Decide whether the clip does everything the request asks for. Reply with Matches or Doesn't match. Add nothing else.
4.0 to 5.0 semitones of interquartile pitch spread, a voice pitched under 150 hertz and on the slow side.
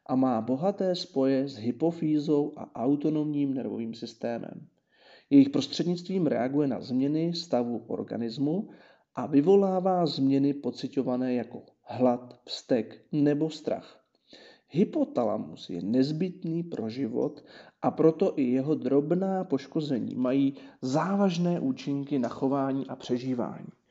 Matches